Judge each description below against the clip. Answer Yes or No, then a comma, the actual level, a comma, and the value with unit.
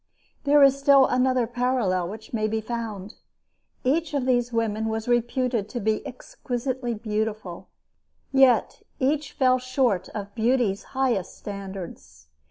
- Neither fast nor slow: No, slow, 130 wpm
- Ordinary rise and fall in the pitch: Yes, average, 3.4 semitones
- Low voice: No, high, 235 Hz